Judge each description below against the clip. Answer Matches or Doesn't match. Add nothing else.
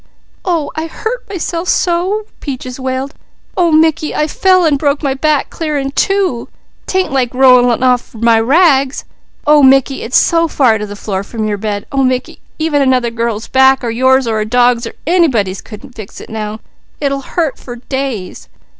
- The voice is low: Doesn't match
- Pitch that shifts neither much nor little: Matches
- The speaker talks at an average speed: Matches